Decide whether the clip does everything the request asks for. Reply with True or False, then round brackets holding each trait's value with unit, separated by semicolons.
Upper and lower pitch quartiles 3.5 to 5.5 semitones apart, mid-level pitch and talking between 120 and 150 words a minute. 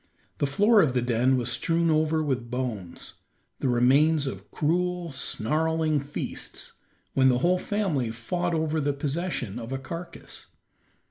True (4.7 semitones; 145 Hz; 145 wpm)